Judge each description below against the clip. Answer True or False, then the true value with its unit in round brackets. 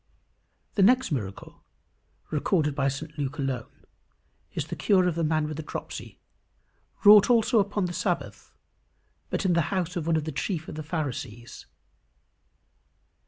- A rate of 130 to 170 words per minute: True (155 wpm)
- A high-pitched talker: False (160 Hz)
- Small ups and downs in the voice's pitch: False (4.3 semitones)